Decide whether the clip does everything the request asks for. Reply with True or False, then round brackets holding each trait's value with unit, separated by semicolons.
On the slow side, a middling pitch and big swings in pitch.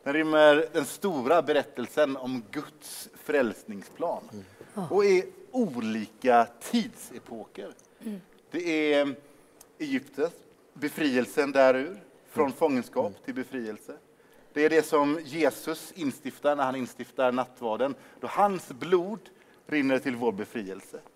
True (110 wpm; 150 Hz; 6.4 semitones)